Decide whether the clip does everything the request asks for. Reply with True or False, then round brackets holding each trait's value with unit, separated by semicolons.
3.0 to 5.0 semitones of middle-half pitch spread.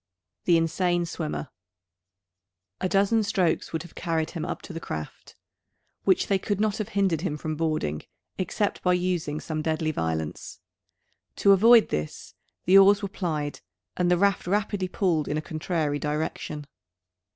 True (3.9 semitones)